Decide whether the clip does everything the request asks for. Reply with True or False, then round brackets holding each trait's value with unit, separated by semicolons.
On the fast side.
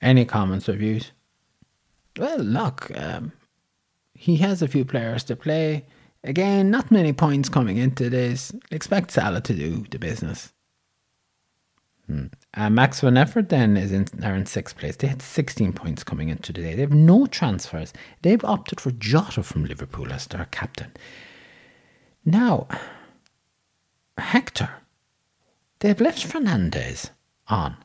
False (140 wpm)